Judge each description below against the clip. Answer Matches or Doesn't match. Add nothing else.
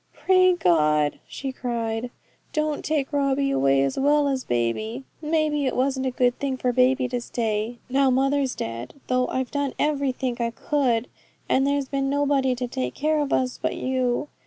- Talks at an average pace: Matches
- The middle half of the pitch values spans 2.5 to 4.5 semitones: Matches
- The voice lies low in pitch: Doesn't match